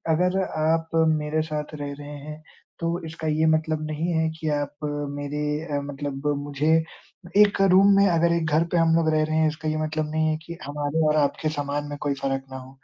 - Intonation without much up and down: Yes, narrow, 1.8 semitones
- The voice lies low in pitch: No, medium, 155 Hz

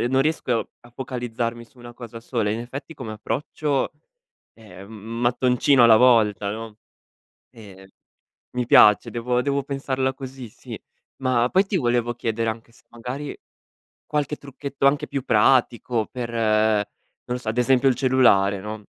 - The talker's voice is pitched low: Yes, low, 120 Hz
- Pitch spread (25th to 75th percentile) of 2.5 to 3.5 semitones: Yes, average, 2.9 semitones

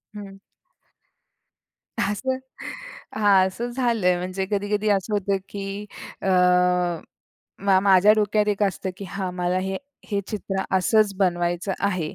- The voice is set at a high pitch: Yes, high, 195 Hz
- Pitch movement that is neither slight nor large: No, narrow, 1.8 semitones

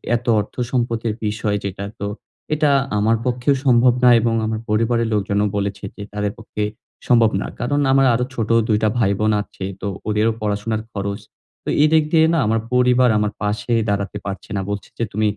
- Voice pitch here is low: Yes, low, 110 Hz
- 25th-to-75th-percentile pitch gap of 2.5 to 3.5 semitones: Yes, average, 2.9 semitones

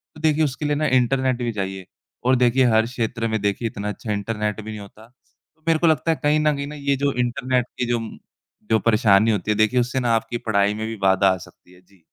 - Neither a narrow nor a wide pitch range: Yes, average, 4.0 semitones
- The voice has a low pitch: Yes, low, 115 Hz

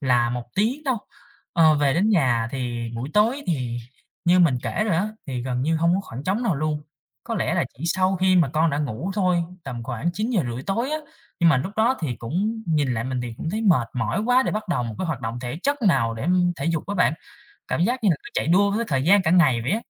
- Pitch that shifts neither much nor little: No, wide, 7.9 semitones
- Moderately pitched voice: Yes, medium, 165 Hz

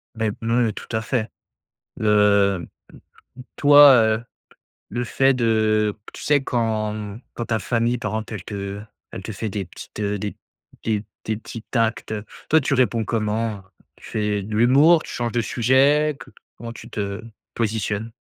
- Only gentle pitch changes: Yes, narrow, 2.3 semitones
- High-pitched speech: No, low, 110 Hz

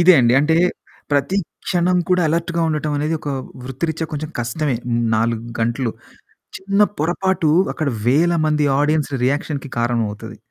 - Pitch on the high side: No, medium, 150 Hz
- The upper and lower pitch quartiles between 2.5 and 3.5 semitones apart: No, average, 4.5 semitones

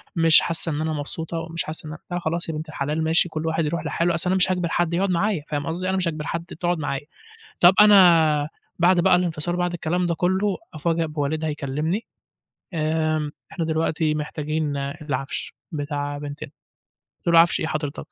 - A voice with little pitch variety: Yes, narrow, 2.3 semitones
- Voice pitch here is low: No, medium, 160 Hz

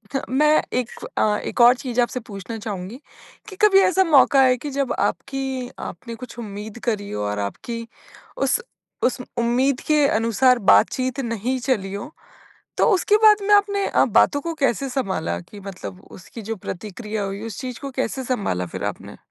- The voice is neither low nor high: No, high, 240 Hz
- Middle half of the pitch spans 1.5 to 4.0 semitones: No, average, 4.7 semitones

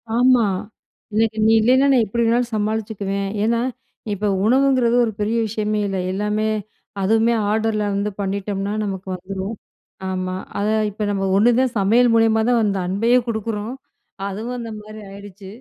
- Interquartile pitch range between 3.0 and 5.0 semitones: No, narrow, 2.6 semitones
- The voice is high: Yes, high, 215 Hz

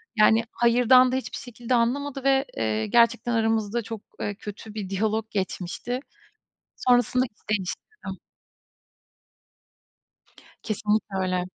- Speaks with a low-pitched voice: No, high, 225 Hz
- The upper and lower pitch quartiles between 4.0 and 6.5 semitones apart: No, average, 3.1 semitones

